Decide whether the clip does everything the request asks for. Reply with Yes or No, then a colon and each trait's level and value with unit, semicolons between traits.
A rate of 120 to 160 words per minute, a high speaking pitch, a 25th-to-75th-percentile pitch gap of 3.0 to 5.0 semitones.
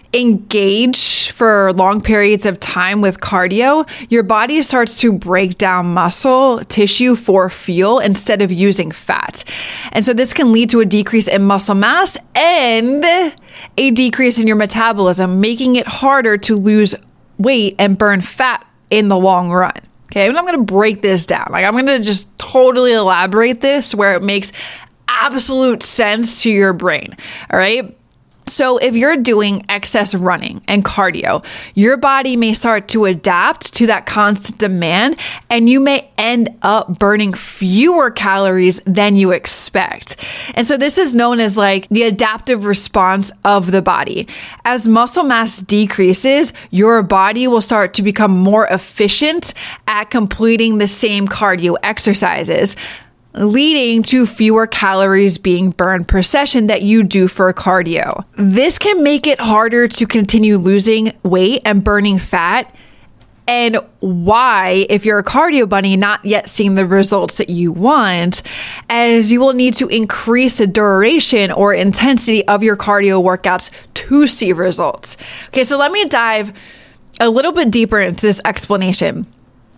Yes: average, 155 wpm; high, 215 Hz; average, 3.6 semitones